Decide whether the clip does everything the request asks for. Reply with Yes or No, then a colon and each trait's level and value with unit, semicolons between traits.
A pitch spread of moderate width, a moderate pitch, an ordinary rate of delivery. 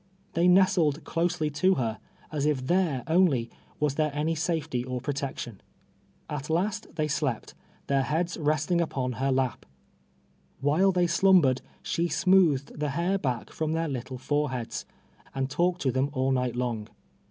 Yes: average, 4.6 semitones; medium, 150 Hz; average, 155 wpm